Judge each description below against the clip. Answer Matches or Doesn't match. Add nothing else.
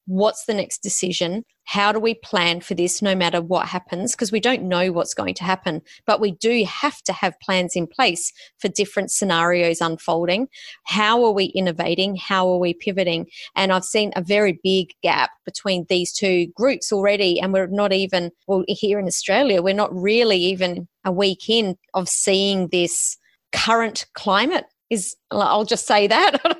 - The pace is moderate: Matches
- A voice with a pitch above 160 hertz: Matches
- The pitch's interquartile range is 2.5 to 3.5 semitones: Matches